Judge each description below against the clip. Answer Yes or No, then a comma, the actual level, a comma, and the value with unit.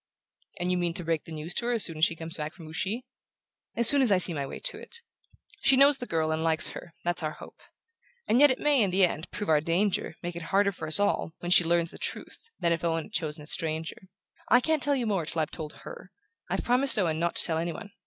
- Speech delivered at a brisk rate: Yes, fast, 270 wpm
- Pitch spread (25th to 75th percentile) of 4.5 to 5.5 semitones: Yes, average, 4.8 semitones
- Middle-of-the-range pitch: Yes, medium, 175 Hz